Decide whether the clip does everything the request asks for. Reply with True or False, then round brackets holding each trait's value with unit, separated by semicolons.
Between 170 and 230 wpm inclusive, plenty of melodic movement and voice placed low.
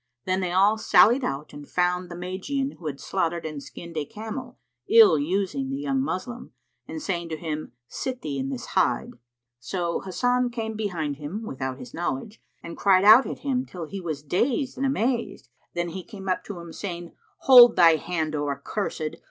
False (190 wpm; 6.8 semitones; 185 Hz)